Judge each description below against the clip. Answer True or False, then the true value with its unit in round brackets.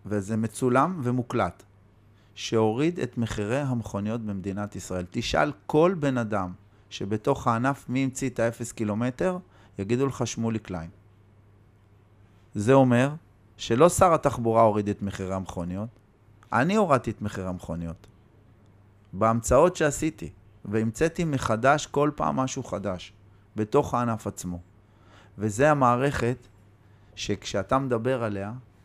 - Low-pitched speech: True (110 Hz)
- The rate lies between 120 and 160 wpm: False (110 wpm)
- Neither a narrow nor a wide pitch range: True (3.7 semitones)